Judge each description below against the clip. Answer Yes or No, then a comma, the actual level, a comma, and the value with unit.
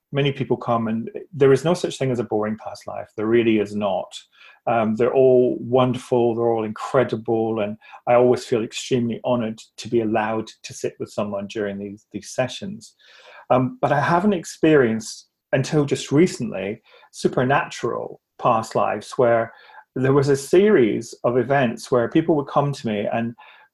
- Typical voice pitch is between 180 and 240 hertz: No, low, 120 Hz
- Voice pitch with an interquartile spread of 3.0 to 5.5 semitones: Yes, average, 3.4 semitones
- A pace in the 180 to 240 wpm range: No, average, 170 wpm